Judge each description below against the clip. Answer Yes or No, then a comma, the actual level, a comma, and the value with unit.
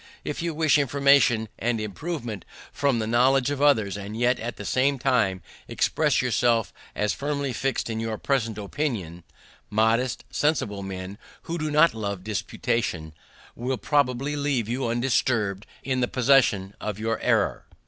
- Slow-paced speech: No, average, 150 wpm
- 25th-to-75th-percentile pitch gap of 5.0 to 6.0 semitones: No, average, 4.6 semitones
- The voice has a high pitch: No, low, 120 Hz